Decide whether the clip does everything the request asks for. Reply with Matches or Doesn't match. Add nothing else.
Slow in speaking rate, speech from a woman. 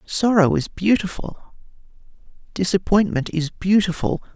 Doesn't match